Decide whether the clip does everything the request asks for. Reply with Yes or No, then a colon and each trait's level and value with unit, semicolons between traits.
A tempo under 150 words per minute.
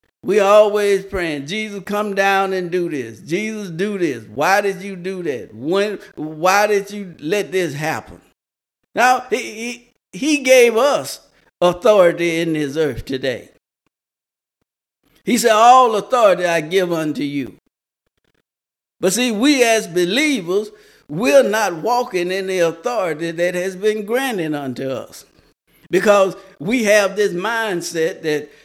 Yes: average, 140 wpm